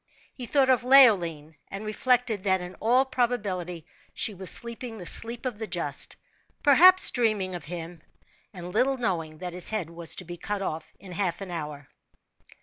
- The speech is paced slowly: No, average, 175 wpm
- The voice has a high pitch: Yes, high, 195 Hz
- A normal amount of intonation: No, wide, 5.7 semitones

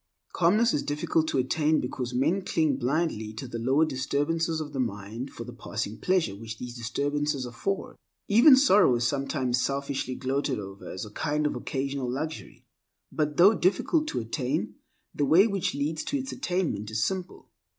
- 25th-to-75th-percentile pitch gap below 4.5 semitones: No, average, 5.0 semitones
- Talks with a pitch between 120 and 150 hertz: Yes, medium, 140 Hz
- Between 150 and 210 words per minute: Yes, average, 170 wpm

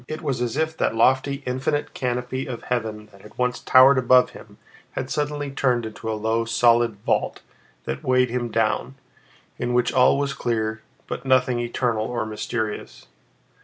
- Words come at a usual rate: Yes, average, 165 wpm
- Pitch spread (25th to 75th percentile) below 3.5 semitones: Yes, narrow, 2.5 semitones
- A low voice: Yes, low, 125 Hz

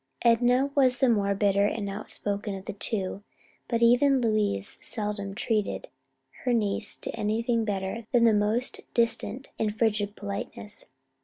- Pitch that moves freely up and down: No, narrow, 2.6 semitones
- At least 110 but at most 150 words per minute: Yes, average, 145 wpm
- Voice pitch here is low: No, high, 215 Hz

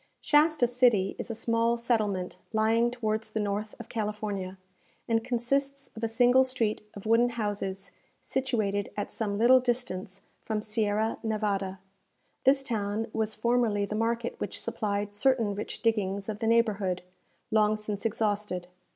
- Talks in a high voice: Yes, high, 220 Hz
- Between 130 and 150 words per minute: Yes, average, 145 wpm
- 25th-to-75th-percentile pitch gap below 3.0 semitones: Yes, narrow, 2.5 semitones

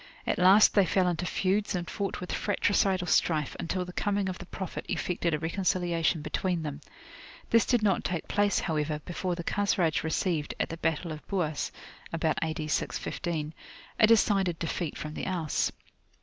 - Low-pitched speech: No, medium, 175 Hz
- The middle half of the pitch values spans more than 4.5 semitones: No, average, 3.1 semitones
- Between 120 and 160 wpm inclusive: No, average, 170 wpm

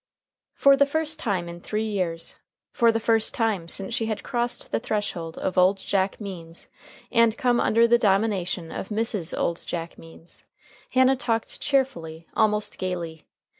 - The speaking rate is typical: Yes, average, 160 wpm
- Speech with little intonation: No, average, 5.0 semitones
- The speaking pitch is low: No, high, 210 Hz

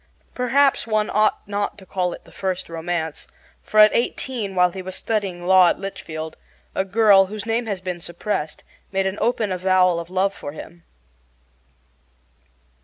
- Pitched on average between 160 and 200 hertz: Yes, high, 190 Hz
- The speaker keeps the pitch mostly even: No, average, 3.1 semitones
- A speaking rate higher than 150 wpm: Yes, average, 165 wpm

